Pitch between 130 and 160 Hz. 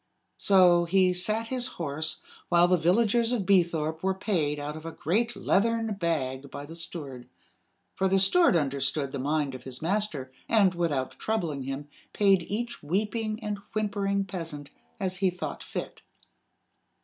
No: medium, 180 Hz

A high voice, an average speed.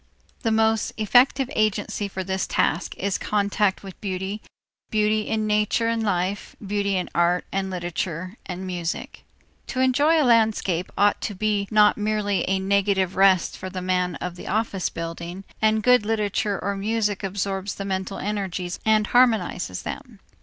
Yes: high, 200 Hz; average, 160 wpm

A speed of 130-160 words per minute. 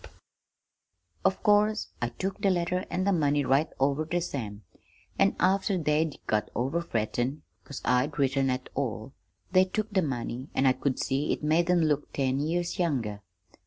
No: average, 170 wpm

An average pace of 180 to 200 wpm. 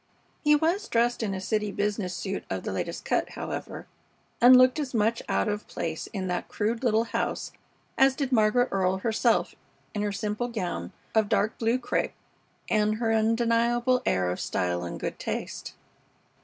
No: average, 170 wpm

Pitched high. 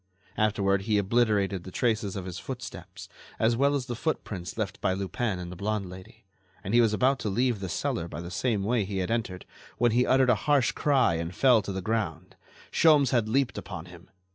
No: low, 105 Hz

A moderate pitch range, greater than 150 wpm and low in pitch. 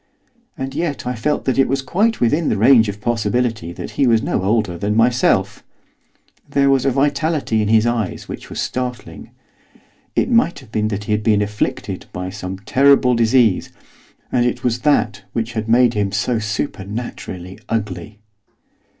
Yes: average, 3.9 semitones; average, 170 wpm; low, 115 Hz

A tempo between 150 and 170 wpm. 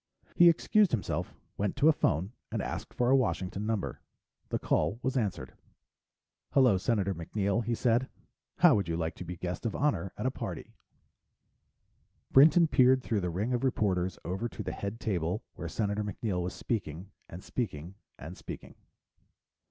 Yes: average, 165 wpm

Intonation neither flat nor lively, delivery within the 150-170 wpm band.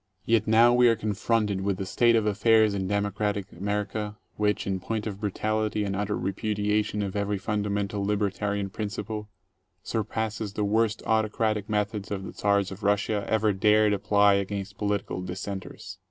No: narrow, 1.3 semitones; average, 155 wpm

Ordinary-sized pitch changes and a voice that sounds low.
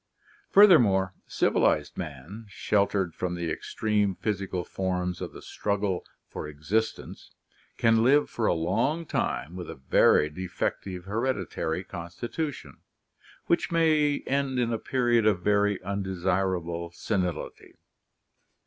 Yes: average, 4.5 semitones; low, 100 Hz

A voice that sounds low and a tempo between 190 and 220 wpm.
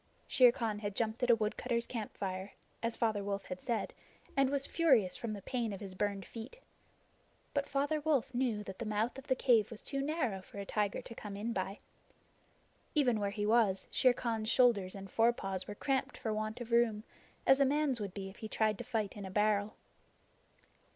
No: high, 220 Hz; fast, 205 wpm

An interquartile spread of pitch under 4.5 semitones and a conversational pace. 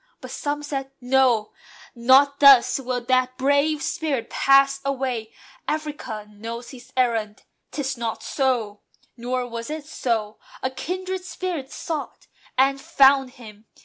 No: average, 3.1 semitones; slow, 130 wpm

